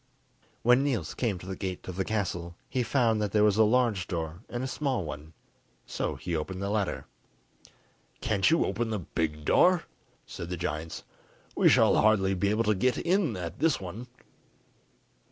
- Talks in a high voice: No, low, 100 Hz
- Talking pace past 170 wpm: Yes, average, 180 wpm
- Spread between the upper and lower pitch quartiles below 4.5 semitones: No, average, 5.1 semitones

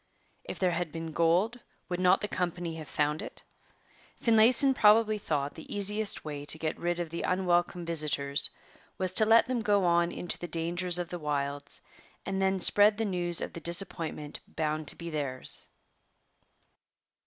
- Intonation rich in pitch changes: No, average, 3.6 semitones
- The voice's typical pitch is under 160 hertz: No, medium, 175 Hz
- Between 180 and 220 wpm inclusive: No, average, 170 wpm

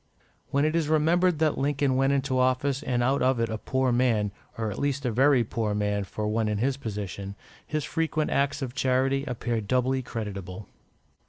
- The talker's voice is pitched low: Yes, low, 130 Hz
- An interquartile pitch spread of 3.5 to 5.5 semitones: Yes, average, 4.2 semitones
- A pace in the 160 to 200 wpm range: Yes, average, 190 wpm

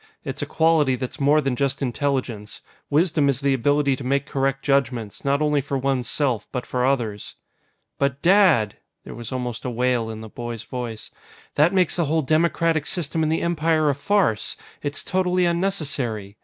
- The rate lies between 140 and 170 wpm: No, average, 180 wpm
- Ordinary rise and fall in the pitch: Yes, average, 4.0 semitones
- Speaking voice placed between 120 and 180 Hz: Yes, medium, 140 Hz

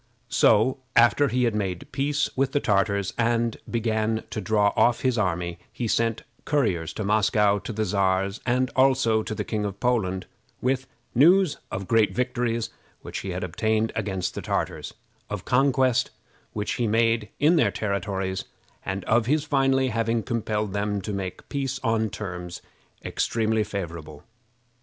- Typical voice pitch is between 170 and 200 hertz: No, low, 110 Hz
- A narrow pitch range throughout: No, average, 3.7 semitones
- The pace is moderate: Yes, average, 155 wpm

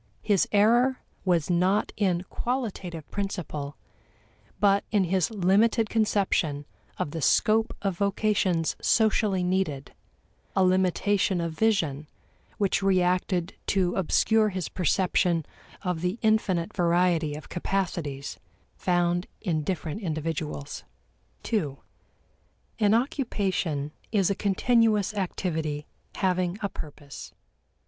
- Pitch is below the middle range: No, medium, 185 Hz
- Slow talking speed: Yes, slow, 105 wpm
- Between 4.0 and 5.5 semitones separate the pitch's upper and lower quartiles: No, average, 3.5 semitones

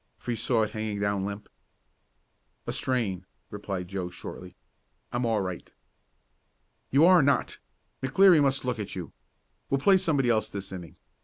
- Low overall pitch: Yes, low, 110 Hz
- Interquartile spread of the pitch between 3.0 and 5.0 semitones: No, wide, 5.5 semitones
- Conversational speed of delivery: Yes, average, 155 wpm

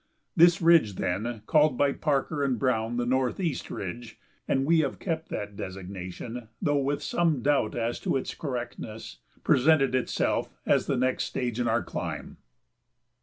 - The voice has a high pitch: No, low, 125 Hz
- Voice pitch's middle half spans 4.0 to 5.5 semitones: Yes, average, 4.3 semitones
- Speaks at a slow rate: No, average, 155 wpm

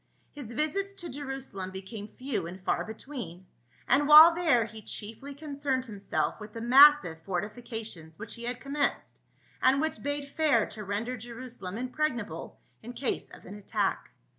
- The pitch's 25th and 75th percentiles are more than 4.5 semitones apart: Yes, wide, 5.4 semitones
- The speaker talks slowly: No, average, 155 wpm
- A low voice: No, high, 240 Hz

